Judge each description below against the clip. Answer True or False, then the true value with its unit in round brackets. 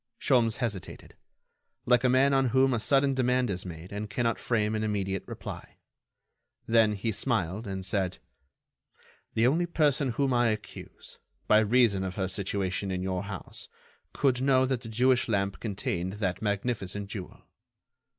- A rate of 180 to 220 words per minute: False (155 wpm)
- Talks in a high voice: False (110 Hz)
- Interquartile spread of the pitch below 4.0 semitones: False (4.4 semitones)